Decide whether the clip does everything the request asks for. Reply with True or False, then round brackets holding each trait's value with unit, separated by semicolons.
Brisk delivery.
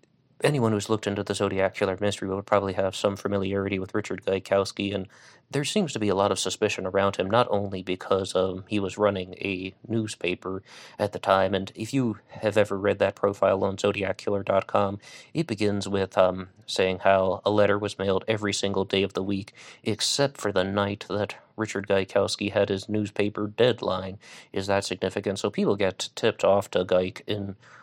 False (190 wpm)